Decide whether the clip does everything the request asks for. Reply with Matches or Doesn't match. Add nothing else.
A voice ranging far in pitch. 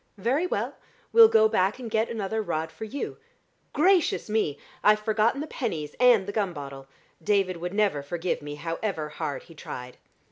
Matches